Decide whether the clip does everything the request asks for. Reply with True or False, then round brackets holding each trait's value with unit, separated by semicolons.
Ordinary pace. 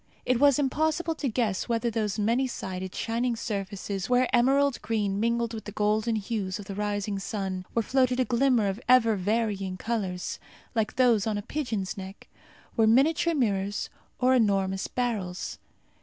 True (160 wpm)